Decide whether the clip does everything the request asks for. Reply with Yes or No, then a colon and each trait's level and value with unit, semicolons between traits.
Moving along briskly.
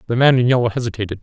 Yes: fast, 245 wpm